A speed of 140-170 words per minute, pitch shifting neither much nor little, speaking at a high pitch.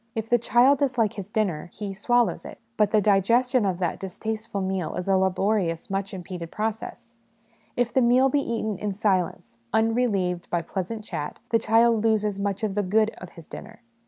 No: average, 185 wpm; average, 3.2 semitones; high, 210 Hz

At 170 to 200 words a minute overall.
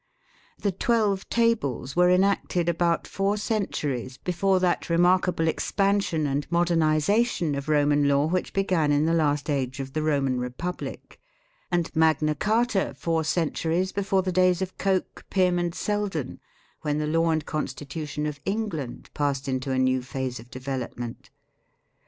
No: average, 150 wpm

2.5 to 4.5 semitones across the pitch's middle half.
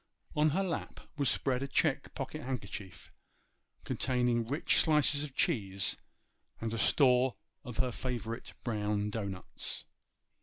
Yes: average, 4.2 semitones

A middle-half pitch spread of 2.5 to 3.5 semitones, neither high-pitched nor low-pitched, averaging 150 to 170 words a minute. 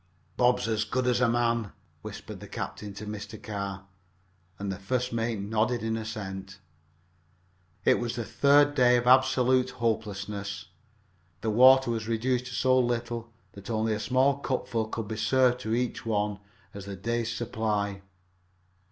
No: average, 2.9 semitones; low, 115 Hz; average, 155 wpm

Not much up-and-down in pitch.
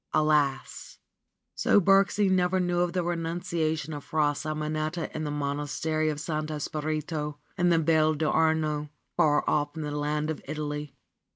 Yes: narrow, 1.8 semitones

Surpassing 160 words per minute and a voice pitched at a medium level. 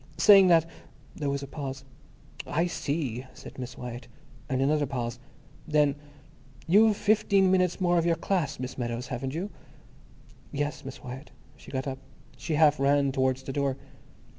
No: average, 155 wpm; medium, 145 Hz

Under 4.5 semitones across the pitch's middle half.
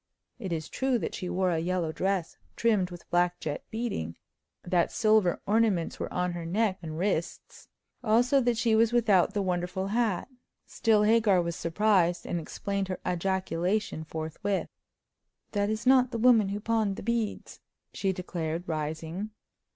Yes: average, 4.0 semitones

